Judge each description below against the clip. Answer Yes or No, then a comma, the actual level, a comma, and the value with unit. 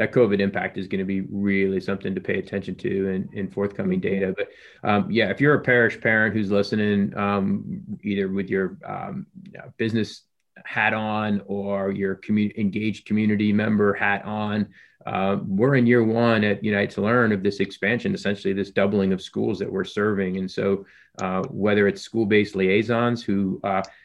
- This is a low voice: Yes, low, 105 Hz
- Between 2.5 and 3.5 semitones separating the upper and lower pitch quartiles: Yes, average, 2.8 semitones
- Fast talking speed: No, average, 190 wpm